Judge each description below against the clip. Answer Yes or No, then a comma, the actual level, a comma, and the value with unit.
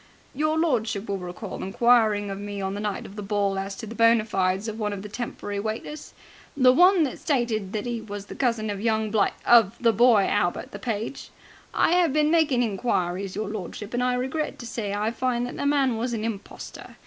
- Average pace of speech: No, fast, 220 wpm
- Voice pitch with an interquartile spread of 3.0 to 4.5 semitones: Yes, average, 3.4 semitones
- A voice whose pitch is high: Yes, high, 220 Hz